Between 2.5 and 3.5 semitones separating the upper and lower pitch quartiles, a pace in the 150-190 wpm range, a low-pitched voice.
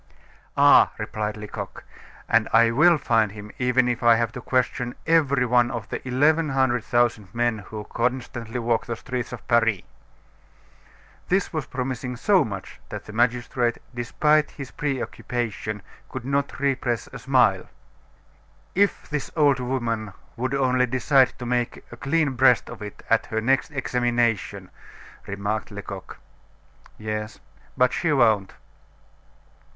No: average, 2.8 semitones; average, 140 wpm; low, 120 Hz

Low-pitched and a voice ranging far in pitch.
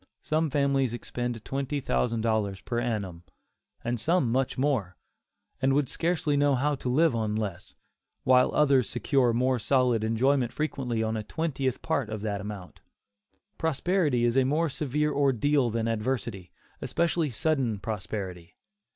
No: low, 125 Hz; average, 4.4 semitones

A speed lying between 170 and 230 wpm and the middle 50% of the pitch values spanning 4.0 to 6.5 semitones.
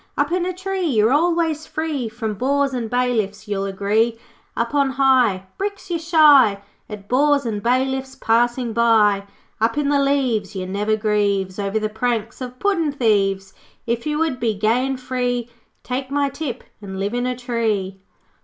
Yes: average, 175 wpm; average, 4.8 semitones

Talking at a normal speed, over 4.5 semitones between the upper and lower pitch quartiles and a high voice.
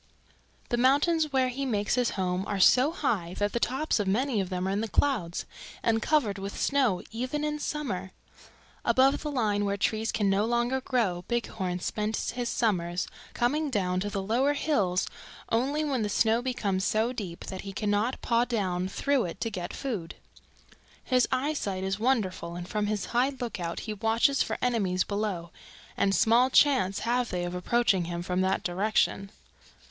Yes: average, 180 wpm; average, 4.9 semitones; high, 220 Hz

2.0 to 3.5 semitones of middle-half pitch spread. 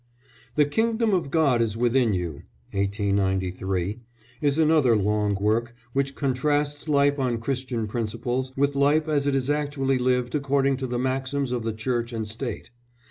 No: average, 4.0 semitones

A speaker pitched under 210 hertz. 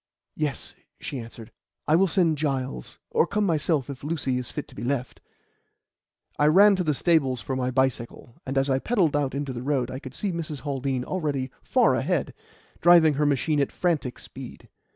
Yes: medium, 140 Hz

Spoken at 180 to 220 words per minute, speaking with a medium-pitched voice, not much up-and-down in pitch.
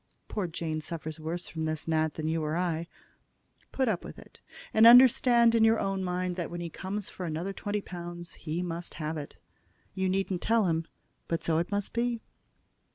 No: average, 195 wpm; medium, 175 Hz; average, 3.9 semitones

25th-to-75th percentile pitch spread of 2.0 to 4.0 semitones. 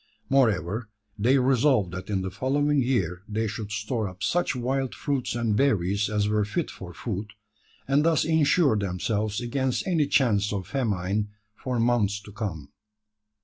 No: average, 4.7 semitones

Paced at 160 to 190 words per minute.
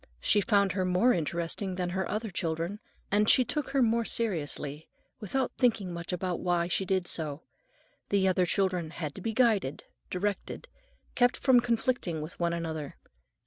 Yes: average, 165 wpm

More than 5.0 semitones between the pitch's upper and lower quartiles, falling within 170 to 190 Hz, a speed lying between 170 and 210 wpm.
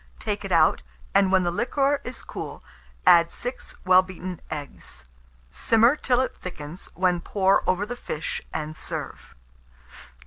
No: wide, 5.4 semitones; medium, 185 Hz; average, 145 wpm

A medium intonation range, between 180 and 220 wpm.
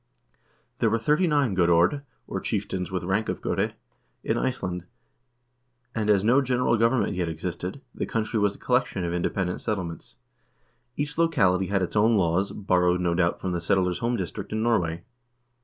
No: average, 4.7 semitones; average, 170 wpm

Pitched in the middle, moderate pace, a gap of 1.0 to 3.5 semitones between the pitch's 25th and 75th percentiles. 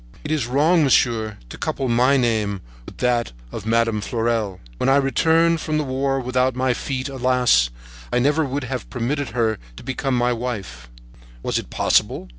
No: low, 125 Hz; average, 180 wpm; average, 2.9 semitones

